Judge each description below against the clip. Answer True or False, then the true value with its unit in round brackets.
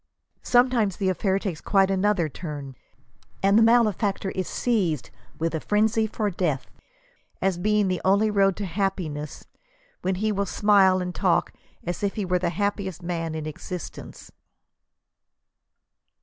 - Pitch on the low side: False (190 Hz)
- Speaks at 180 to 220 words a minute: False (150 wpm)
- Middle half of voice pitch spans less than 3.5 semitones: True (3.1 semitones)